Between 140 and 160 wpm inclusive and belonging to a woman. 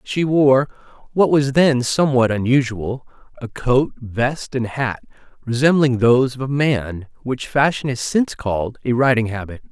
No: average, 155 wpm; male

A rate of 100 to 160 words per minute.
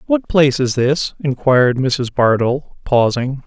Yes: average, 140 wpm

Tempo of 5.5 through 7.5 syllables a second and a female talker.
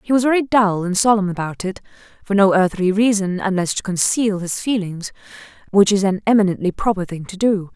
Yes: 5.6 syllables/s; female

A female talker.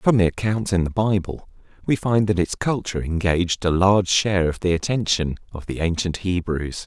No: male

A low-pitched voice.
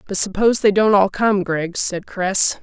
No: high, 200 Hz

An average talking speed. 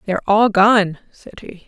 Yes: average, 180 wpm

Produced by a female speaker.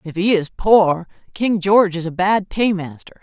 Yes: female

